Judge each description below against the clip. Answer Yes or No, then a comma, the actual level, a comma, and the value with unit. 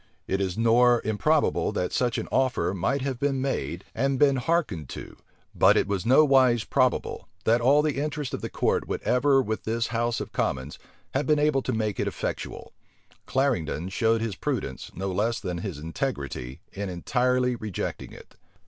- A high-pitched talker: No, low, 120 Hz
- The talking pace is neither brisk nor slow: Yes, average, 175 wpm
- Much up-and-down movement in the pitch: Yes, wide, 5.7 semitones